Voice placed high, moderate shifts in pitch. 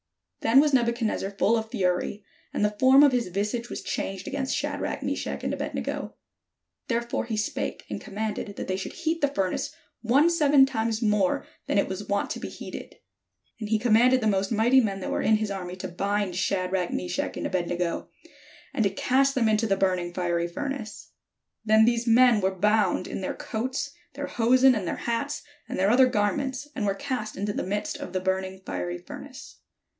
Yes: high, 215 Hz; average, 4.5 semitones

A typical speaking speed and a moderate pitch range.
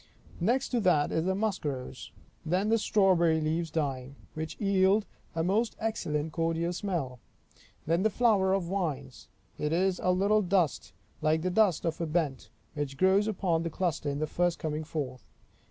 Yes: average, 170 wpm; average, 3.9 semitones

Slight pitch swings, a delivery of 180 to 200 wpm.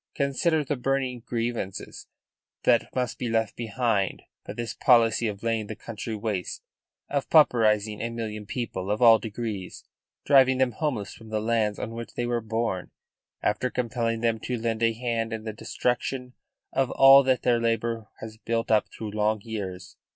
No: narrow, 2.2 semitones; average, 170 wpm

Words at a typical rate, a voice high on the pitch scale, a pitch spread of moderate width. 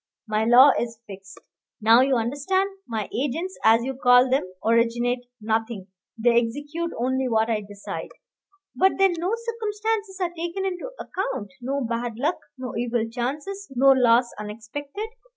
No: average, 150 wpm; very high, 255 Hz; wide, 6.9 semitones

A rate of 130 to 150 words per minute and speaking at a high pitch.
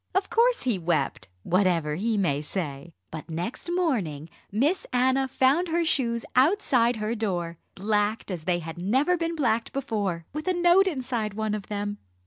No: average, 165 wpm; high, 220 Hz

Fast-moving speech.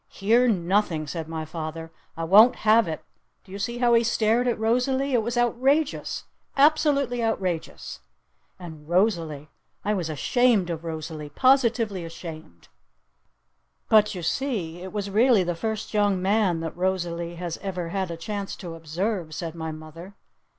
No: average, 155 wpm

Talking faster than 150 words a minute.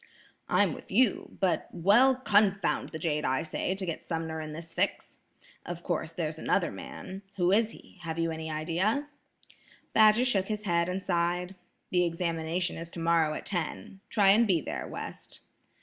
Yes: average, 165 wpm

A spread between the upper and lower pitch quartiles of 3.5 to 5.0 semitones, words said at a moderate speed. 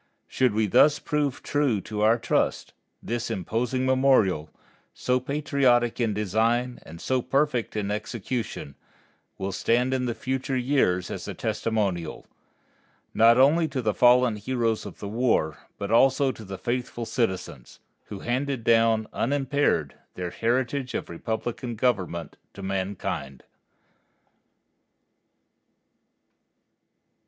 No: average, 3.8 semitones; slow, 120 wpm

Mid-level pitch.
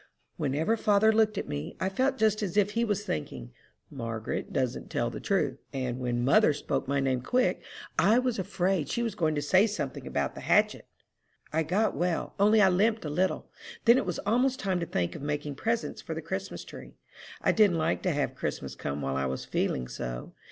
Yes: medium, 180 Hz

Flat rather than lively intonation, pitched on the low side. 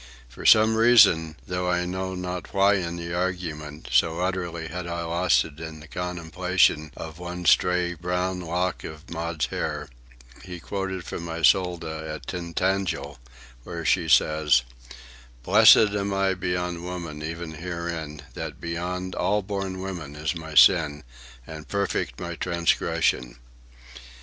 Yes: narrow, 2.2 semitones; very low, 85 Hz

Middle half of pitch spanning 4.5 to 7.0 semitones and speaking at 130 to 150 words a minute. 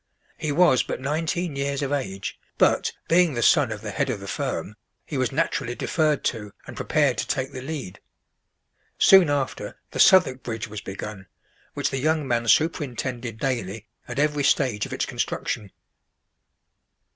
No: average, 4.9 semitones; average, 165 wpm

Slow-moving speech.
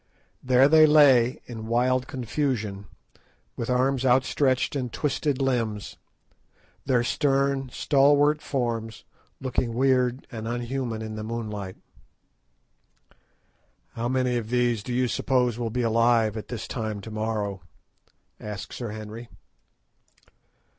Yes: slow, 120 wpm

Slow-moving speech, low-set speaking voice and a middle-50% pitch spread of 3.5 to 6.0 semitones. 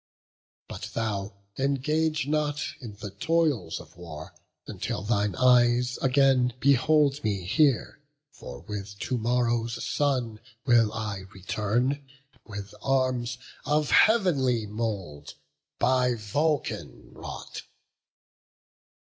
Yes: slow, 100 wpm; low, 120 Hz; average, 4.9 semitones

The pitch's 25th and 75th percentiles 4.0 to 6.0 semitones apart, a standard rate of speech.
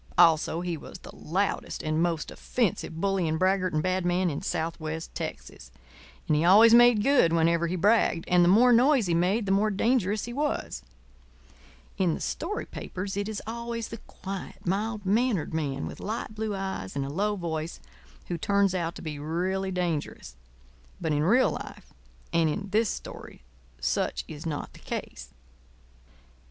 Yes: average, 4.5 semitones; average, 170 wpm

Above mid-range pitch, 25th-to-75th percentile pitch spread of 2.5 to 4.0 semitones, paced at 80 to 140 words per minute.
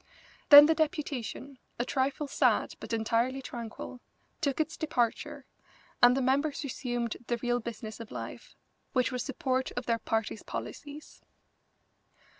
Yes: very high, 255 Hz; average, 3.1 semitones; slow, 135 wpm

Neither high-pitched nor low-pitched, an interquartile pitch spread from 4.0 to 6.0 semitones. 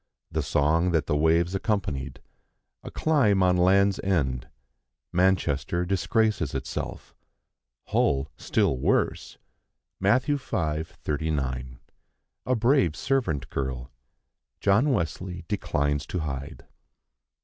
No: very low, 85 Hz; wide, 5.4 semitones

